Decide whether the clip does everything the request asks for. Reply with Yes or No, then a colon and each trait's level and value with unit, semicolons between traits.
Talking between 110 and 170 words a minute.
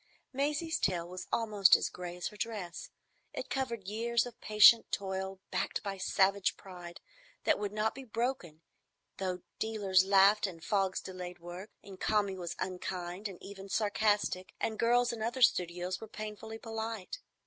Yes: average, 160 wpm